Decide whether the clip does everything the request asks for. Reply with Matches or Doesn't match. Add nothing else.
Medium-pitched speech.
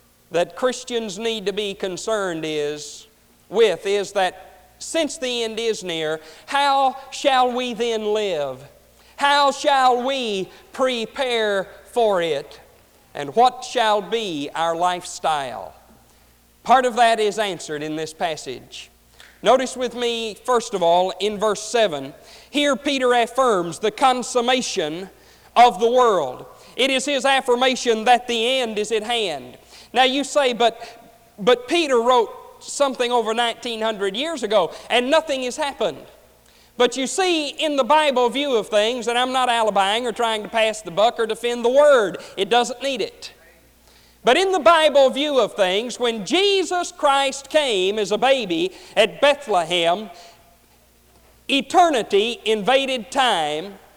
Doesn't match